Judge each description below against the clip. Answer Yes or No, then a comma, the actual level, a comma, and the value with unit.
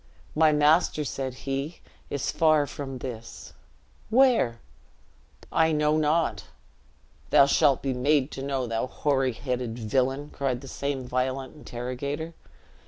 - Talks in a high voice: No, low, 135 Hz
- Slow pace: Yes, slow, 125 wpm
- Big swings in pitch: No, average, 2.8 semitones